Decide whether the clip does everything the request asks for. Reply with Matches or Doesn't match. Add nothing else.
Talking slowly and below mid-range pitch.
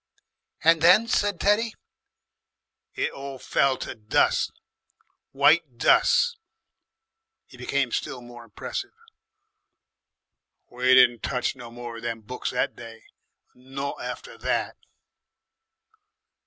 Matches